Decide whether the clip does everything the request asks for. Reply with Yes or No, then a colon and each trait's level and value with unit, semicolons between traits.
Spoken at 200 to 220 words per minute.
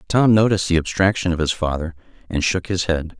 Yes: fast, 205 wpm